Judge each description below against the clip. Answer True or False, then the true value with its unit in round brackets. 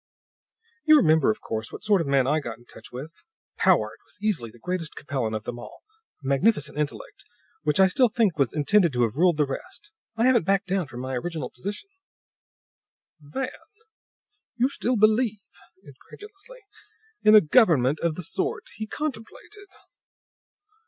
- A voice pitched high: False (170 Hz)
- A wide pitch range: True (8.1 semitones)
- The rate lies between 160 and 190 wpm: True (165 wpm)